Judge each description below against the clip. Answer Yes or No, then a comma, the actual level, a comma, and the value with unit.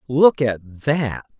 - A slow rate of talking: Yes, slow, 130 wpm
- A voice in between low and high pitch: No, low, 130 Hz